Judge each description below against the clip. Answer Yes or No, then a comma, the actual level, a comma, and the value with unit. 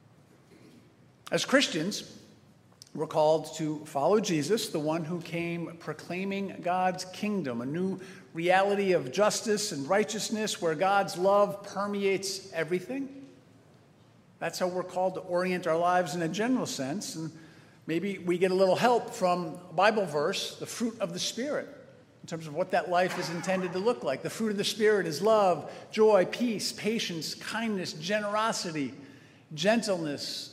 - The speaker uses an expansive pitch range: No, average, 4.0 semitones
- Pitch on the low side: No, medium, 185 Hz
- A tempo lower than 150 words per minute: No, average, 155 wpm